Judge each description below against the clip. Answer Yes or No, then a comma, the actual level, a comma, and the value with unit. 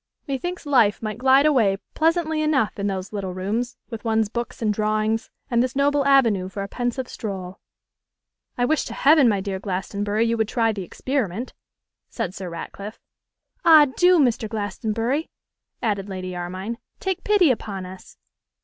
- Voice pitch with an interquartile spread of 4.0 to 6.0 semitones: Yes, average, 5.2 semitones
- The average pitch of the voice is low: No, high, 225 Hz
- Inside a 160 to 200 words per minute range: Yes, average, 165 wpm